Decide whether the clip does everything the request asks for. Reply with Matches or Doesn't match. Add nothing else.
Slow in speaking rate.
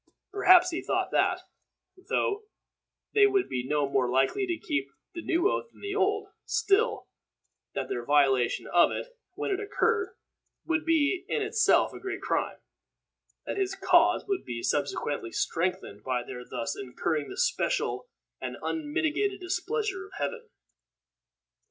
Doesn't match